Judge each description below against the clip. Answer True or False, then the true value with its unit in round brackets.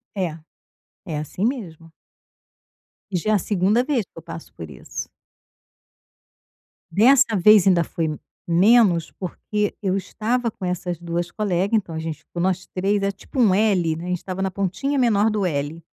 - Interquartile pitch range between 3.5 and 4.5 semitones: True (3.8 semitones)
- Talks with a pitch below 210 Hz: True (190 Hz)